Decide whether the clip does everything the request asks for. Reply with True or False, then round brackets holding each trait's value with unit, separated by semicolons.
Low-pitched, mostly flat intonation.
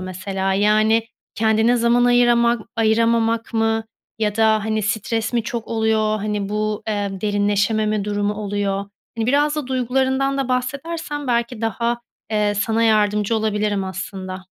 False (220 Hz; 2.3 semitones)